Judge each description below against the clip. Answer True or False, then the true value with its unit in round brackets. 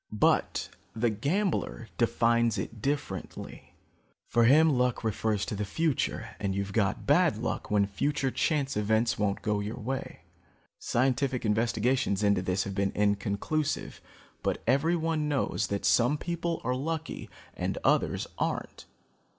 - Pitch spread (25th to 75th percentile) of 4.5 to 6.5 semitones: True (5.6 semitones)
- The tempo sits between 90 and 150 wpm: True (135 wpm)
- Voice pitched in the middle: False (115 Hz)